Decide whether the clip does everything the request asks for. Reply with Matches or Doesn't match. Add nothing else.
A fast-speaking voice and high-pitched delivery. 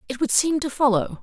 Matches